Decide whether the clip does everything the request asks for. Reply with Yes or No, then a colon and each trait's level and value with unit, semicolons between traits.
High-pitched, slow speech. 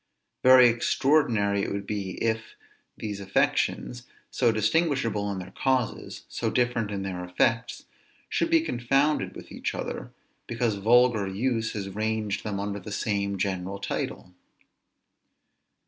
No: low, 110 Hz; slow, 130 wpm